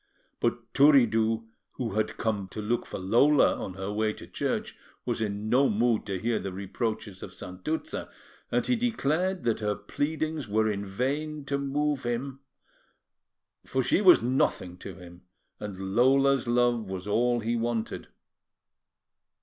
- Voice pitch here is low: Yes, low, 115 Hz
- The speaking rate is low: No, average, 150 wpm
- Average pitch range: Yes, average, 4.9 semitones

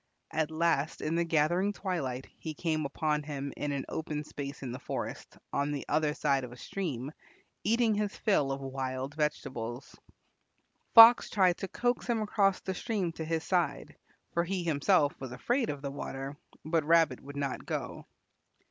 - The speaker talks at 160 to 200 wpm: Yes, average, 175 wpm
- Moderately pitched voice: Yes, medium, 155 Hz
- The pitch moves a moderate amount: Yes, average, 4.5 semitones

